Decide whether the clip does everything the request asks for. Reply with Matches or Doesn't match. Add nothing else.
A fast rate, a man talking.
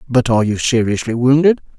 Doesn't match